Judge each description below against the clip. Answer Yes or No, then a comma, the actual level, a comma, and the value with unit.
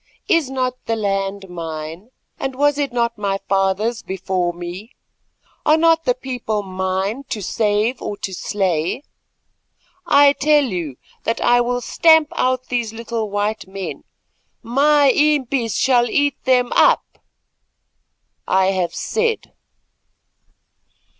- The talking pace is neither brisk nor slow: No, slow, 125 wpm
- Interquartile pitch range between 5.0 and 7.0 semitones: Yes, wide, 5.6 semitones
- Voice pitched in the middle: No, high, 230 Hz